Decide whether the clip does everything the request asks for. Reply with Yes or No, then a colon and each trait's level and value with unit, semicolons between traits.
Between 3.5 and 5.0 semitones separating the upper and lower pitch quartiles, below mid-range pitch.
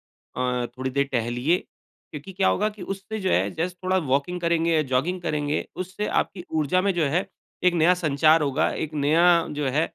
No: average, 4.6 semitones; medium, 160 Hz